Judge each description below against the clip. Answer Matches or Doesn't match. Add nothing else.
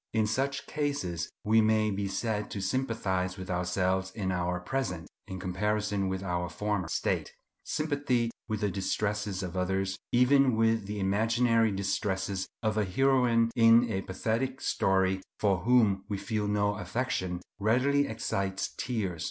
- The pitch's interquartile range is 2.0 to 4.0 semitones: Matches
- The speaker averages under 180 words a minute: Matches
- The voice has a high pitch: Doesn't match